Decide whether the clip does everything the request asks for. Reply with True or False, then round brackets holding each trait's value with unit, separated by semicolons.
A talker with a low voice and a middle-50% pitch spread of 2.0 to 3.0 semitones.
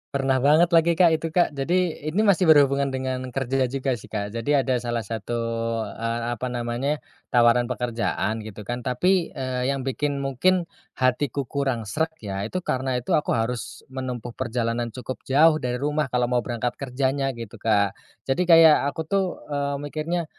False (130 Hz; 3.7 semitones)